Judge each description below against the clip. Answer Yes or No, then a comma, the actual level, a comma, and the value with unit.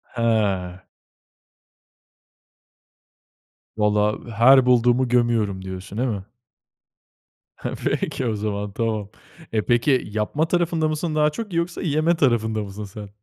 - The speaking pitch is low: Yes, low, 115 Hz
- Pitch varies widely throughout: Yes, wide, 5.8 semitones